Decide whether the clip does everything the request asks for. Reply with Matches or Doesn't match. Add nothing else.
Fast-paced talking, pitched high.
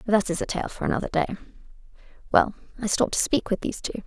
Matches